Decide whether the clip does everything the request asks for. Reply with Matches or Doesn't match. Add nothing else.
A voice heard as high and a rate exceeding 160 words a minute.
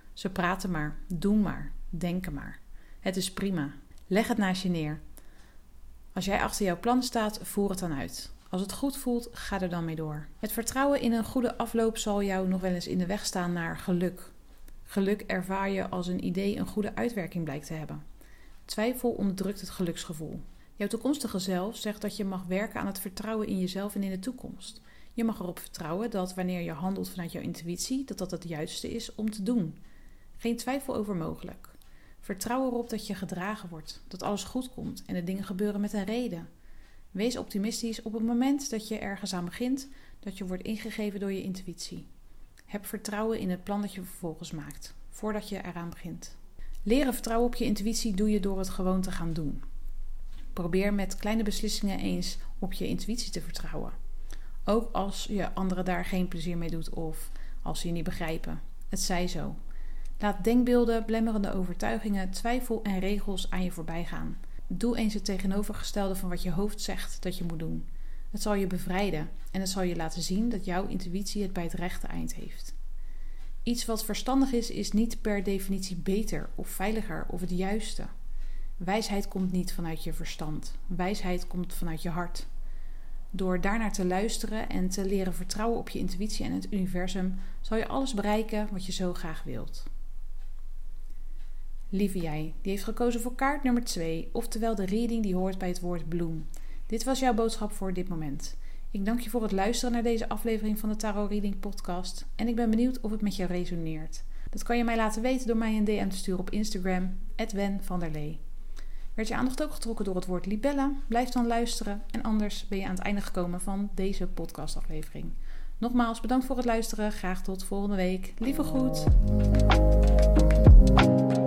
Matches